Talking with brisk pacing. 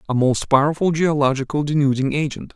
No: average, 140 wpm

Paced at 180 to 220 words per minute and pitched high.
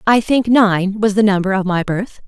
No: fast, 235 wpm; high, 205 Hz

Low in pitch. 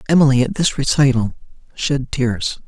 Yes: low, 130 Hz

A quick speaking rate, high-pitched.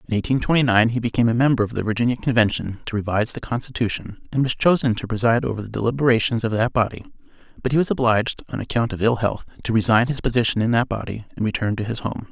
No: fast, 235 wpm; low, 115 Hz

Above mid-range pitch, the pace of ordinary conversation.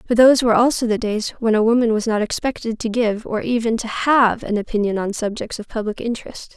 No: high, 225 Hz; fast, 230 wpm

